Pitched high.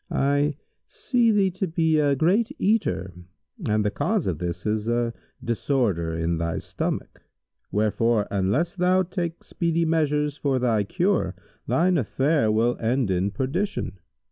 No: low, 135 Hz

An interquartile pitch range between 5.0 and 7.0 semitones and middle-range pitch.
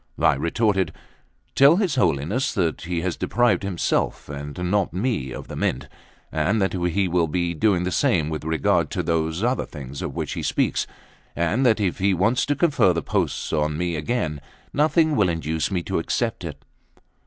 No: wide, 5.5 semitones; very low, 90 Hz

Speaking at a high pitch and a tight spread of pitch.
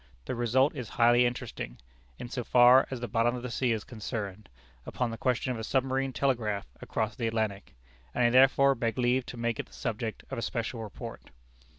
No: low, 120 Hz; narrow, 2.2 semitones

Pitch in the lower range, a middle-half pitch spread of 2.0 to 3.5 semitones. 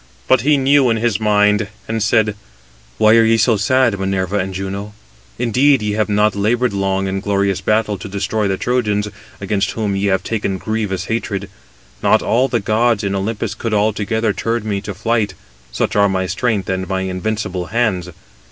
Yes: low, 105 Hz; narrow, 2.5 semitones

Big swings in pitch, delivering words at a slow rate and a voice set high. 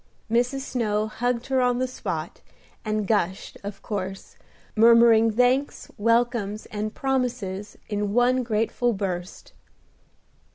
No: average, 3.0 semitones; slow, 115 wpm; high, 230 Hz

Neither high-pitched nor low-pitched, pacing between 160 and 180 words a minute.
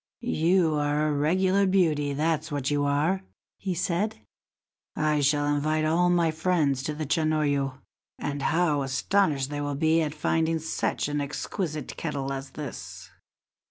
No: medium, 150 Hz; average, 150 wpm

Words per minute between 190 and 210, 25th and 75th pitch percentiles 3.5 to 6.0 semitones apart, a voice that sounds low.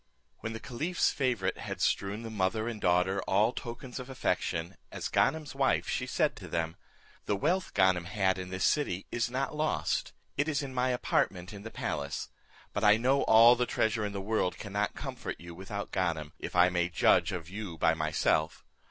Yes: average, 195 wpm; wide, 5.5 semitones; low, 105 Hz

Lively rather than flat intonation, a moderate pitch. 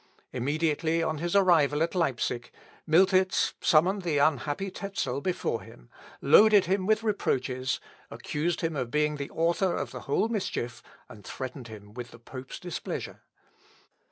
Yes: wide, 6.0 semitones; medium, 155 Hz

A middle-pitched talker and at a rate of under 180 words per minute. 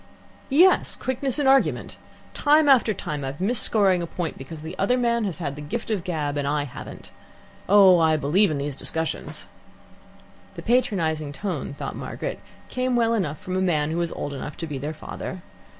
No: medium, 175 Hz; average, 195 wpm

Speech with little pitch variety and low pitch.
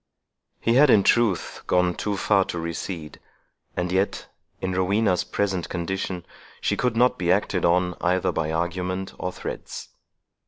Yes: narrow, 2.2 semitones; very low, 90 Hz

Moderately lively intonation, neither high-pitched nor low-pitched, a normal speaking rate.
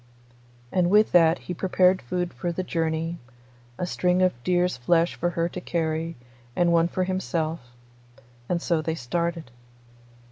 No: narrow, 1.6 semitones; medium, 170 Hz; average, 150 wpm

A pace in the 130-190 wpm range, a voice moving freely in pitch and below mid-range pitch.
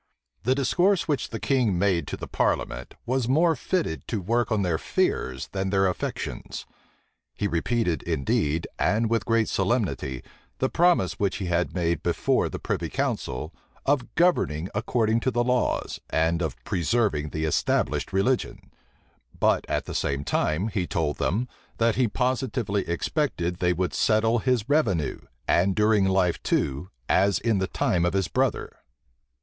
Yes: average, 155 wpm; wide, 5.9 semitones; low, 100 Hz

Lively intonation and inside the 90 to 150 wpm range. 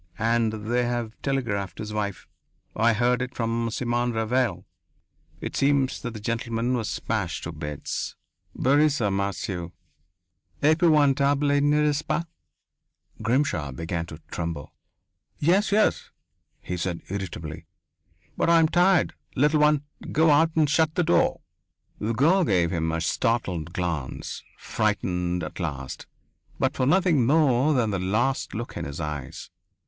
Yes: wide, 7.9 semitones; average, 140 wpm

